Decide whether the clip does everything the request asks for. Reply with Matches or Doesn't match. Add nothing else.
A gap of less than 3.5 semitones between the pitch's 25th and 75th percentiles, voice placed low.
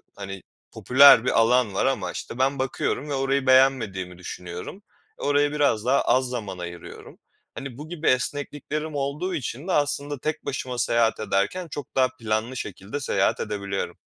Doesn't match